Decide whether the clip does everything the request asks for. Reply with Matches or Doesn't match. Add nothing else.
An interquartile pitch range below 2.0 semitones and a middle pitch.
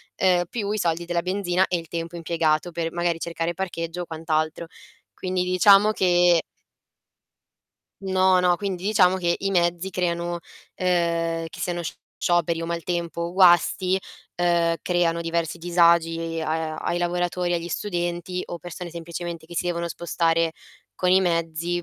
Matches